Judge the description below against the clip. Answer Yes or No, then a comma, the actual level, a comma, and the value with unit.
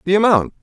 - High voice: No, medium, 180 Hz